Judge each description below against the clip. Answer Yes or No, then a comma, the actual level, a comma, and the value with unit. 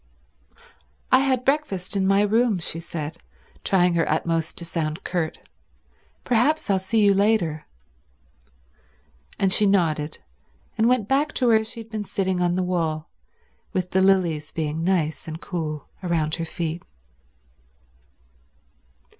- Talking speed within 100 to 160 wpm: Yes, average, 140 wpm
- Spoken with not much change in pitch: No, average, 4.6 semitones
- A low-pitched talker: No, medium, 185 Hz